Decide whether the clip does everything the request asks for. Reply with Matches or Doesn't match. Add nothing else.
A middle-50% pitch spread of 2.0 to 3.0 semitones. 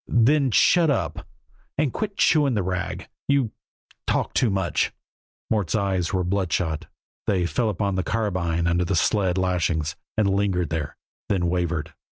Doesn't match